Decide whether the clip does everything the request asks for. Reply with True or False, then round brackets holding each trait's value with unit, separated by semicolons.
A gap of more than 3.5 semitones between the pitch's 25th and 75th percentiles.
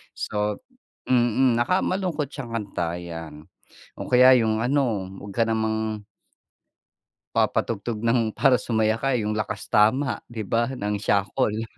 False (3.1 semitones)